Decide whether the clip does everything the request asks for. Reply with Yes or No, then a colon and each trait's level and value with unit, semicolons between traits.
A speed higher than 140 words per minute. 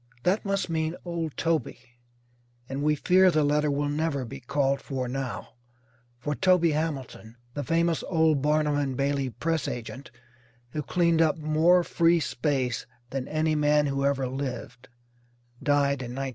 Yes: average, 155 wpm